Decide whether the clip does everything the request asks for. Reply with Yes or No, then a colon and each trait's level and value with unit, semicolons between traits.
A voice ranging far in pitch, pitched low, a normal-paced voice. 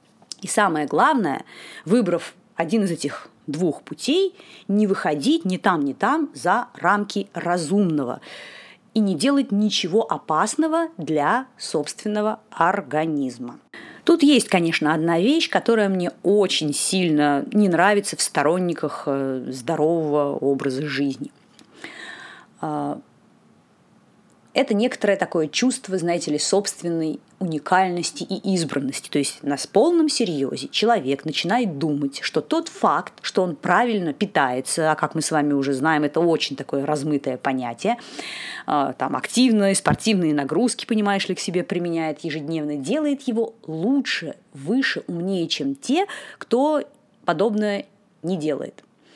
No: wide, 6.6 semitones; medium, 180 Hz; average, 120 wpm